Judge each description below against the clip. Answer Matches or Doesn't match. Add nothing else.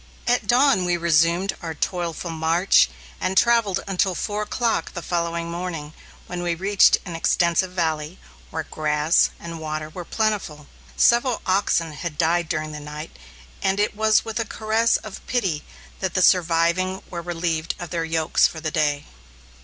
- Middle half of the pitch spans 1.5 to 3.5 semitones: Matches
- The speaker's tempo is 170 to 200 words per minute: Doesn't match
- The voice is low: Doesn't match